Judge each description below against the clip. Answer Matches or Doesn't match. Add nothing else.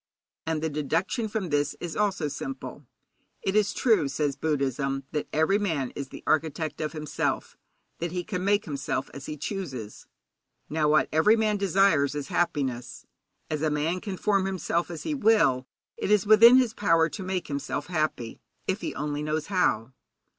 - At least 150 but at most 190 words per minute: Matches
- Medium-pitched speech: Matches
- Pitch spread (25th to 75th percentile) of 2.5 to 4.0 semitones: Doesn't match